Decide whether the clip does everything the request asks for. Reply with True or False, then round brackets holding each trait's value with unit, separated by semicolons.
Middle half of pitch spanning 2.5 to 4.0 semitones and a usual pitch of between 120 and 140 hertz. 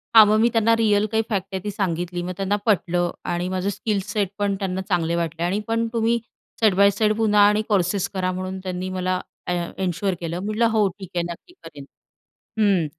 False (2.8 semitones; 195 Hz)